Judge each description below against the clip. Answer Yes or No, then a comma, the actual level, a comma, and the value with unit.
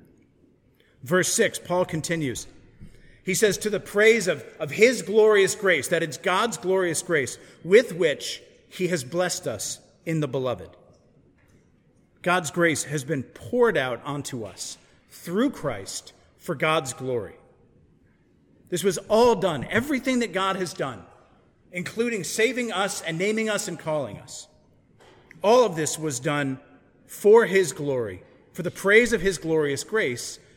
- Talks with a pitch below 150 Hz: No, medium, 180 Hz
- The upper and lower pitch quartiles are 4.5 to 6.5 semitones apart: Yes, wide, 5.5 semitones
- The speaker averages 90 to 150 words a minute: Yes, average, 145 wpm